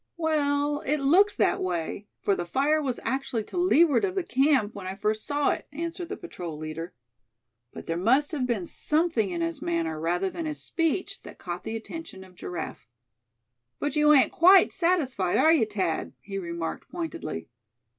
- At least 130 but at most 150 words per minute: No, average, 180 wpm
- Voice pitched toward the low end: No, very high, 260 Hz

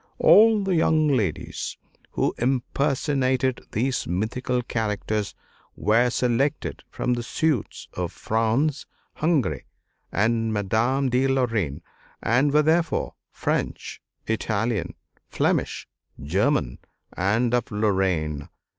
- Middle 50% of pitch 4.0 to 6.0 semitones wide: Yes, average, 4.4 semitones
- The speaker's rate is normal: No, slow, 100 wpm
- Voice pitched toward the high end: No, low, 120 Hz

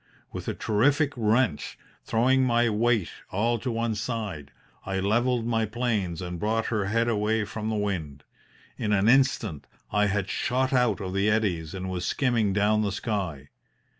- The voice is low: Yes, low, 105 Hz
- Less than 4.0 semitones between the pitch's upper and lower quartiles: Yes, average, 3.3 semitones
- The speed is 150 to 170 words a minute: Yes, average, 165 wpm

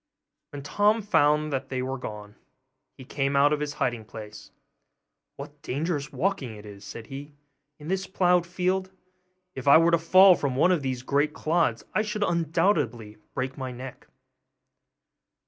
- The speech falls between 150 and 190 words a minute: Yes, average, 160 wpm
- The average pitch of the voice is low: No, medium, 145 Hz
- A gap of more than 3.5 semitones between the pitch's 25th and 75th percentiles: Yes, average, 5.0 semitones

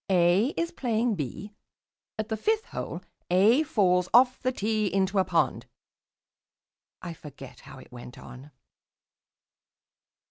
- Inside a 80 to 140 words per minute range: Yes, slow, 135 wpm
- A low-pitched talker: No, high, 200 Hz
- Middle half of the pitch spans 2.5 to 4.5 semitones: No, wide, 5.4 semitones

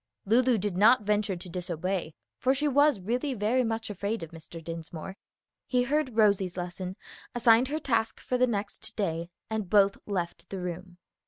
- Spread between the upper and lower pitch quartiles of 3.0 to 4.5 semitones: No, average, 5.1 semitones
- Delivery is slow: No, average, 170 wpm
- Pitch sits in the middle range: No, high, 205 Hz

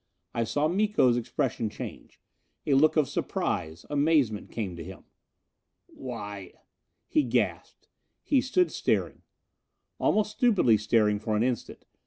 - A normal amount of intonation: No, wide, 7.5 semitones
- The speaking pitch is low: Yes, low, 120 Hz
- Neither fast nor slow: No, slow, 130 wpm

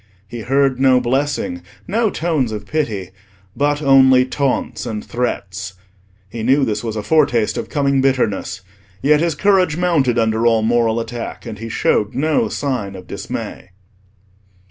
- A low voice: Yes, low, 125 Hz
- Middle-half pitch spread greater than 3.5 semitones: Yes, average, 4.4 semitones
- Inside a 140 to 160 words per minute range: Yes, average, 150 wpm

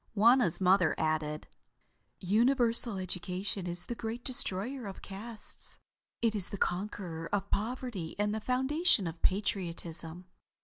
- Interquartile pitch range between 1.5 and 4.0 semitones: No, average, 4.7 semitones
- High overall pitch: Yes, high, 200 Hz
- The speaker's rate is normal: No, slow, 125 wpm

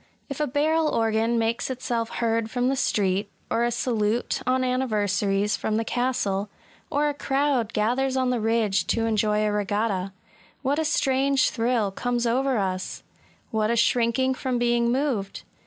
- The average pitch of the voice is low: No, high, 235 Hz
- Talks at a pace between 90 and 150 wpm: No, average, 175 wpm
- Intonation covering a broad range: No, average, 3.4 semitones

